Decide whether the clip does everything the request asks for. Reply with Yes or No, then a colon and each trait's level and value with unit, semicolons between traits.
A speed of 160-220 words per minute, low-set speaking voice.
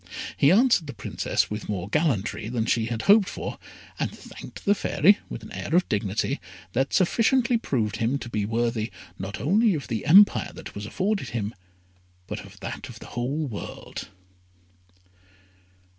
Yes: average, 165 wpm; low, 125 Hz